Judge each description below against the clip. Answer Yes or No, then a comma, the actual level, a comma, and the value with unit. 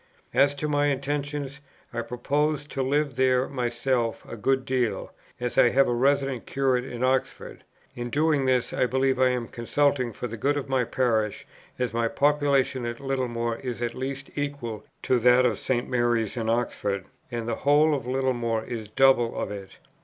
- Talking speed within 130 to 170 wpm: No, average, 180 wpm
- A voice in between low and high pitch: No, low, 130 Hz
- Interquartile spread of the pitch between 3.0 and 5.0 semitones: No, narrow, 2.6 semitones